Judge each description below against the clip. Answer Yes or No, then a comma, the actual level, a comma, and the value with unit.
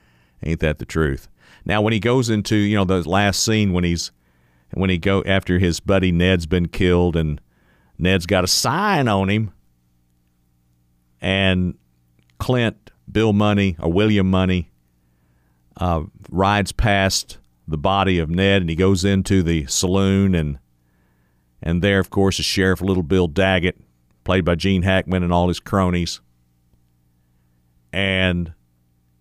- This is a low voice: Yes, very low, 90 Hz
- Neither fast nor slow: Yes, average, 145 wpm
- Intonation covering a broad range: Yes, wide, 8.2 semitones